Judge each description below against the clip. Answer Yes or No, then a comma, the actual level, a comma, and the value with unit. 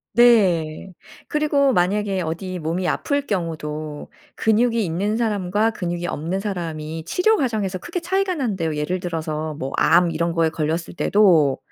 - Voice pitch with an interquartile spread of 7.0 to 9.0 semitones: No, average, 5.3 semitones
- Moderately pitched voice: Yes, medium, 180 Hz